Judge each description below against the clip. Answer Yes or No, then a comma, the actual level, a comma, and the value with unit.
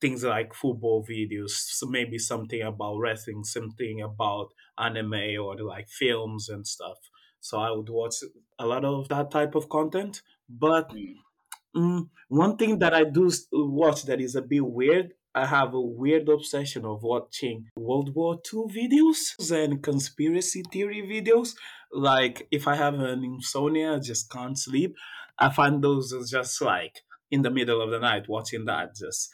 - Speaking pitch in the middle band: No, low, 130 Hz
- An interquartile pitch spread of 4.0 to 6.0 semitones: Yes, average, 5.2 semitones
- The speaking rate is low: No, average, 160 wpm